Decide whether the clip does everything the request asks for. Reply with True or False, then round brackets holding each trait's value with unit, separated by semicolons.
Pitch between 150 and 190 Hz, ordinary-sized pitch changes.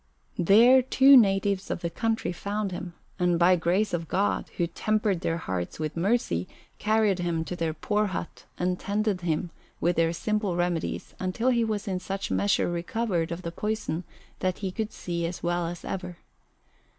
True (185 Hz; 3.7 semitones)